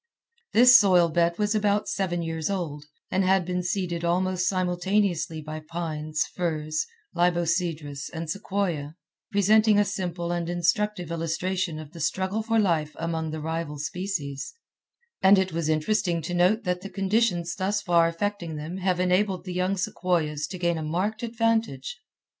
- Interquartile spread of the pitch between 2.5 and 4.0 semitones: Yes, average, 3.2 semitones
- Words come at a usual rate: Yes, average, 155 wpm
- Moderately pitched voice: Yes, medium, 175 Hz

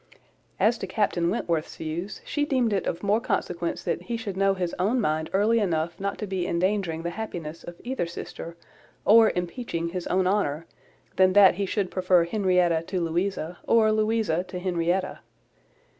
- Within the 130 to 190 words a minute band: Yes, average, 175 wpm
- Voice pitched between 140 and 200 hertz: Yes, medium, 185 Hz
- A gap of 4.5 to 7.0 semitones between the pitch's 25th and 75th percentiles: No, average, 3.4 semitones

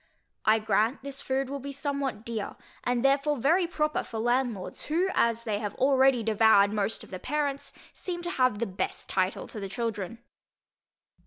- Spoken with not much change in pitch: No, average, 4.5 semitones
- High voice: Yes, high, 245 Hz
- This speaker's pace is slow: No, average, 175 wpm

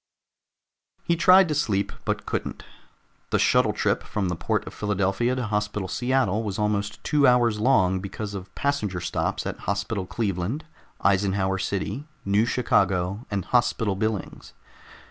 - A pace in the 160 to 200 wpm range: No, average, 145 wpm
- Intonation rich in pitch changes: No, average, 3.9 semitones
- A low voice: Yes, low, 105 Hz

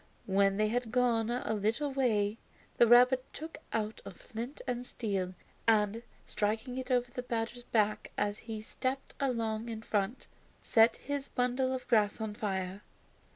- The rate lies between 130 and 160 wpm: Yes, average, 155 wpm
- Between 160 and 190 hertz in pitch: No, high, 225 Hz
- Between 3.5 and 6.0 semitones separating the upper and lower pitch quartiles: No, average, 2.8 semitones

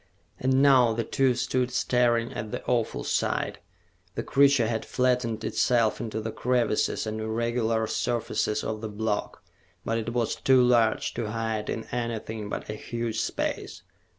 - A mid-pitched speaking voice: No, low, 115 Hz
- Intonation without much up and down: Yes, narrow, 1.9 semitones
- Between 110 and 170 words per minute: Yes, average, 155 wpm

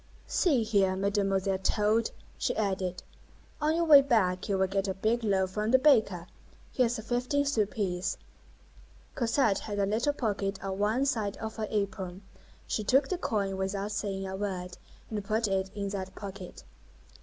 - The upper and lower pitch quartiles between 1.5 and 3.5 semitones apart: Yes, average, 2.9 semitones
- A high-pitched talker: Yes, high, 205 Hz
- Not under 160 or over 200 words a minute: Yes, average, 170 wpm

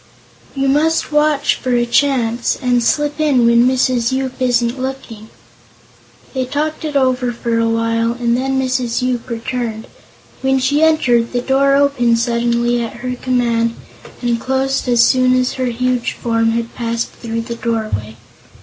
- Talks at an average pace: Yes, average, 160 wpm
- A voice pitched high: Yes, high, 245 Hz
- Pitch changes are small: Yes, narrow, 2.2 semitones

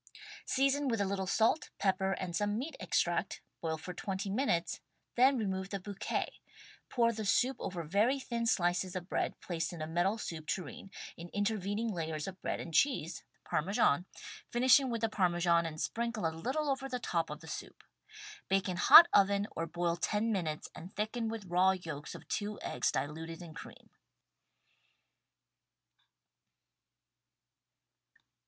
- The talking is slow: No, average, 165 wpm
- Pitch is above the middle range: Yes, high, 195 Hz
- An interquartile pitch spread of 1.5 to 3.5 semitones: No, average, 4.8 semitones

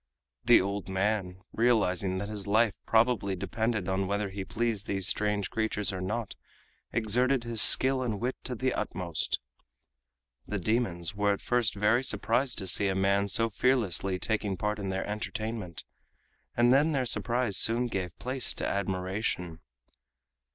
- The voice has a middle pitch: No, low, 105 Hz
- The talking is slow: No, average, 155 wpm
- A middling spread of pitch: Yes, average, 3.5 semitones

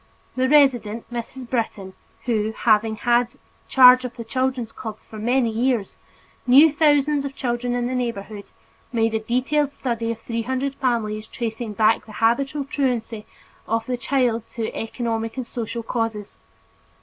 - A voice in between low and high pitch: No, high, 235 Hz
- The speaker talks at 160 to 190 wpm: No, average, 150 wpm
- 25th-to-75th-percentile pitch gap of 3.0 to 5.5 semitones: No, narrow, 2.4 semitones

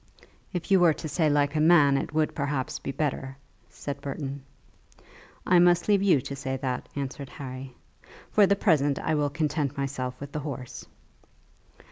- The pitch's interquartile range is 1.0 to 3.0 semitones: Yes, narrow, 2.5 semitones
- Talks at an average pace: Yes, average, 170 wpm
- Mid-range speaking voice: Yes, medium, 145 Hz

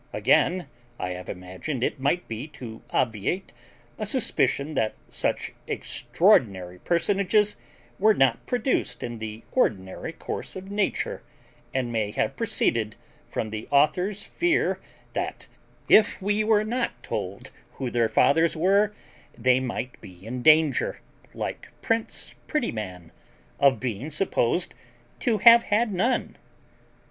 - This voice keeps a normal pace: No, slow, 125 wpm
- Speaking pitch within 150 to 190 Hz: No, medium, 140 Hz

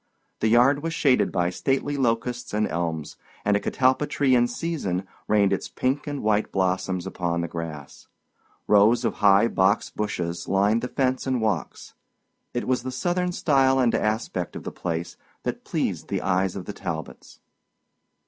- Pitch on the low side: Yes, low, 105 Hz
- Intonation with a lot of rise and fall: Yes, wide, 5.9 semitones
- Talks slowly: No, average, 165 wpm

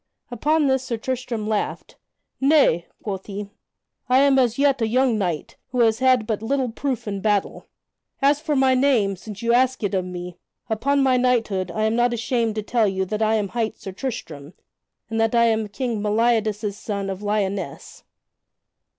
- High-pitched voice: Yes, high, 225 Hz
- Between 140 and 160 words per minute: No, average, 185 wpm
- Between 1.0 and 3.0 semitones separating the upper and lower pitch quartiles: No, average, 3.8 semitones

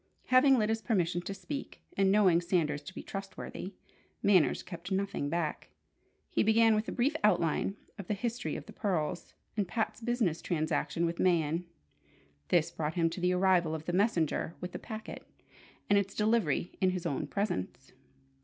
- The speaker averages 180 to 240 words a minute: No, average, 170 wpm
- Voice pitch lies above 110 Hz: Yes, medium, 185 Hz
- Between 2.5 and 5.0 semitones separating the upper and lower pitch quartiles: Yes, average, 4.0 semitones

